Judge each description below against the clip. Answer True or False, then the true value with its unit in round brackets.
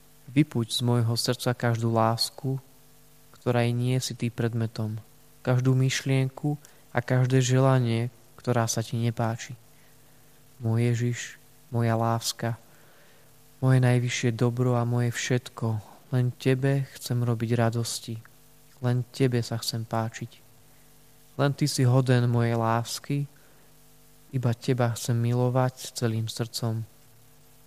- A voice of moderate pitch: False (125 Hz)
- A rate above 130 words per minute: False (115 wpm)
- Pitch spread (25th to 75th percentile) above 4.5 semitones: False (2.7 semitones)